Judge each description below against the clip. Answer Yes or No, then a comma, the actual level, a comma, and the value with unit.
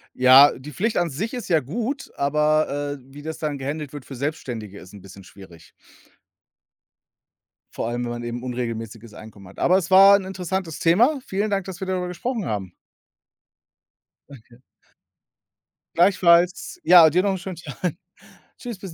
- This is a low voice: No, medium, 155 Hz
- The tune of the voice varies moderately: No, wide, 7.4 semitones